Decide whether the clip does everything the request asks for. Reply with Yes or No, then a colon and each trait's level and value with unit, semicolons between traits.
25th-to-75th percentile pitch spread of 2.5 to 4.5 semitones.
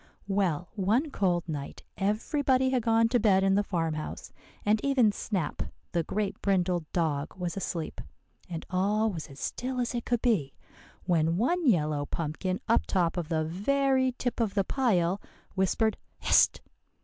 No: average, 5.3 semitones